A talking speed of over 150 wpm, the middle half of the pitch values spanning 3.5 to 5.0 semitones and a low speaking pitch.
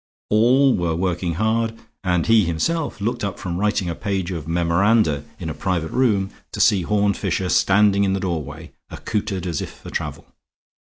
Yes: average, 175 wpm; average, 3.8 semitones; very low, 95 Hz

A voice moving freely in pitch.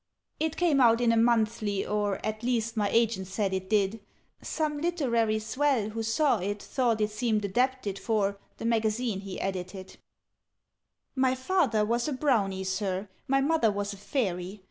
No: average, 3.8 semitones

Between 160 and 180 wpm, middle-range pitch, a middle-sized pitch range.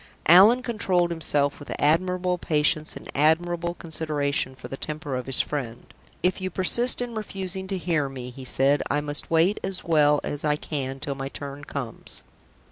Yes: average, 175 wpm; medium, 155 Hz; average, 4.2 semitones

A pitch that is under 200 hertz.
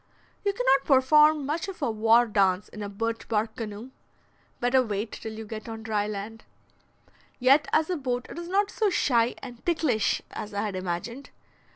No: high, 235 Hz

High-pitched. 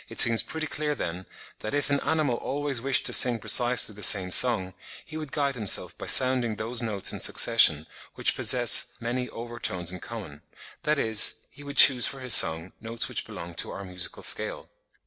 No: low, 115 Hz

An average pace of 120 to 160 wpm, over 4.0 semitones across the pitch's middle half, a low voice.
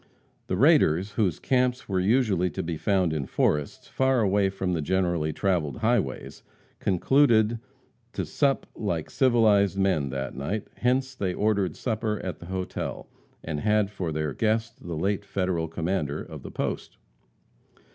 Yes: average, 150 wpm; average, 4.6 semitones; very low, 95 Hz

